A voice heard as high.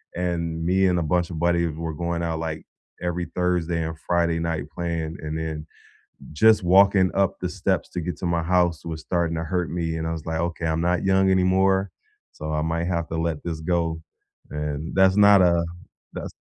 No: very low, 85 Hz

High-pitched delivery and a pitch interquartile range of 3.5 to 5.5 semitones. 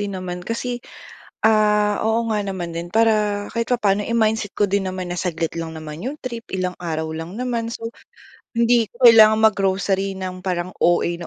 Yes: high, 200 Hz; average, 3.9 semitones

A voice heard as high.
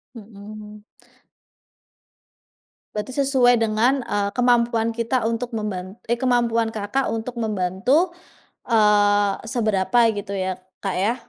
Yes: high, 220 Hz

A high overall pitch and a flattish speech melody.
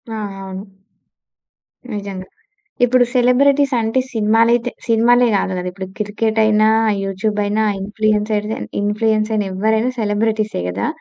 Yes: high, 215 Hz; narrow, 1.8 semitones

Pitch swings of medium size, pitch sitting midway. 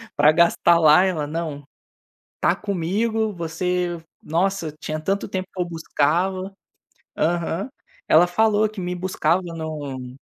Yes: average, 3.0 semitones; medium, 175 Hz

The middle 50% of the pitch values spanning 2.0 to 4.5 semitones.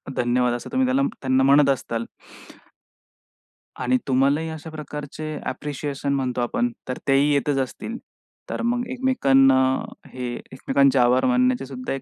Yes: average, 3.4 semitones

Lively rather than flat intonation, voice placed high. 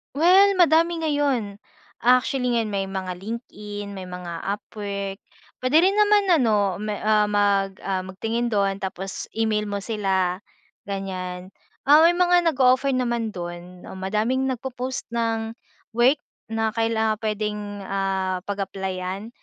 No: average, 4.6 semitones; high, 215 Hz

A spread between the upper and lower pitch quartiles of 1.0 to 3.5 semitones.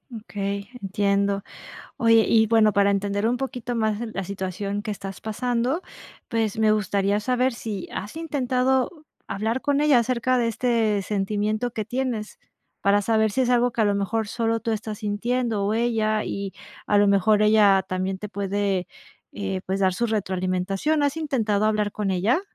Yes: average, 2.9 semitones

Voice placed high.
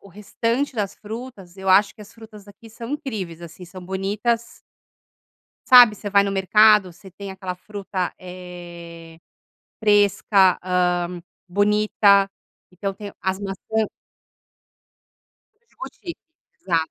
Yes: high, 195 Hz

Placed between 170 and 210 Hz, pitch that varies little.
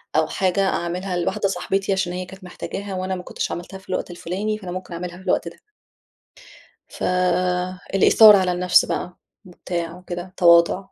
Yes: medium, 185 Hz; narrow, 1.5 semitones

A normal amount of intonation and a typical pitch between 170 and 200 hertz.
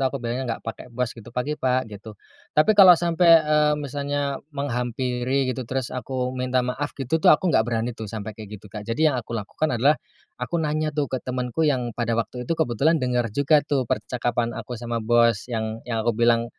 No: average, 3.4 semitones; low, 125 Hz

